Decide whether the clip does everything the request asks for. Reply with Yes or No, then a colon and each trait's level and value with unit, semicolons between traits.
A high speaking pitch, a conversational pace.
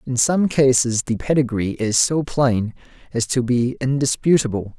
No: low, 130 Hz; average, 150 wpm